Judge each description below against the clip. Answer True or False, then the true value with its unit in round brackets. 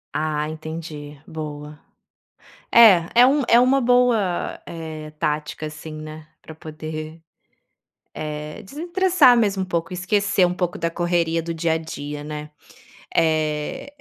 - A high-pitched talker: False (160 Hz)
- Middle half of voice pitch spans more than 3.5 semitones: True (3.9 semitones)